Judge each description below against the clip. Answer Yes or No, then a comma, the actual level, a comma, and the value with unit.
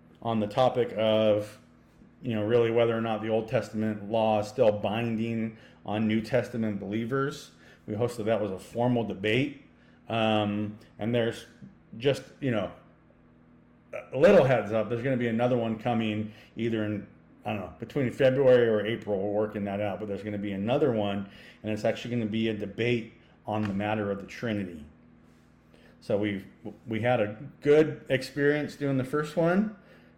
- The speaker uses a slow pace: No, average, 180 wpm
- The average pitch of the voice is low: Yes, low, 110 Hz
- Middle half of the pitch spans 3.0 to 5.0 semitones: No, narrow, 2.4 semitones